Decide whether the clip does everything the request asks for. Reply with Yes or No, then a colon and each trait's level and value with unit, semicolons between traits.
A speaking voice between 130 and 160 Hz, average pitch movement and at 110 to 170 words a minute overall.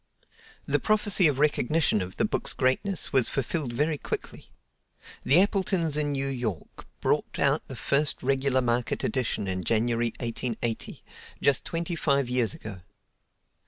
Yes: low, 135 Hz; average, 4.4 semitones; average, 140 wpm